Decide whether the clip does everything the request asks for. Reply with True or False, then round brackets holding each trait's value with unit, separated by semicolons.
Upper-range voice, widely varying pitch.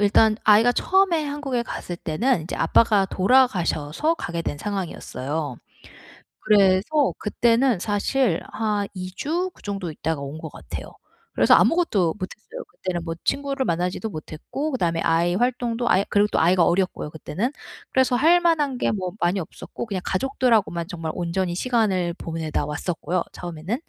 True (200 Hz; 6.6 semitones)